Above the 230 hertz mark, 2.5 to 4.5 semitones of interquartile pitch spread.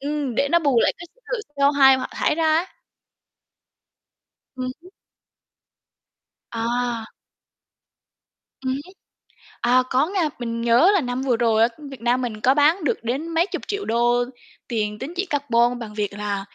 Yes: very high, 255 Hz; average, 4.2 semitones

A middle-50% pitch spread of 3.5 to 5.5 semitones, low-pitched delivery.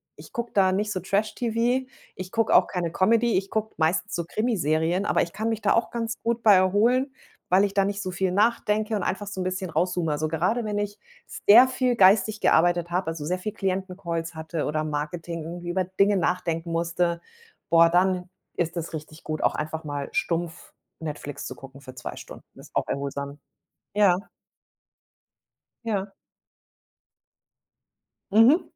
No: average, 4.1 semitones; medium, 185 Hz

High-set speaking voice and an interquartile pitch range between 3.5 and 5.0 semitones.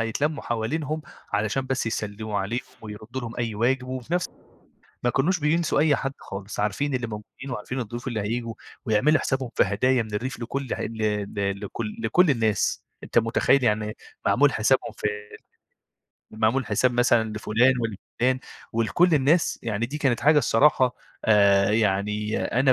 No: low, 120 Hz; average, 3.8 semitones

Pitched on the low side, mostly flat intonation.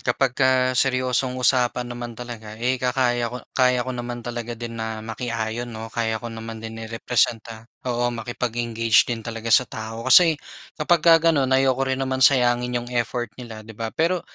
Yes: low, 120 Hz; narrow, 2.1 semitones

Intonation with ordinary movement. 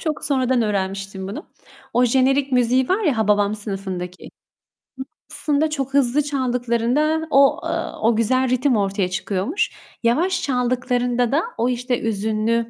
Yes: average, 4.1 semitones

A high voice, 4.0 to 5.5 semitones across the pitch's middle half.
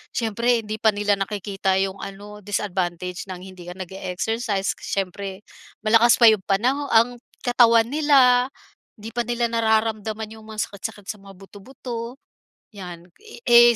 No: high, 215 Hz; average, 3.1 semitones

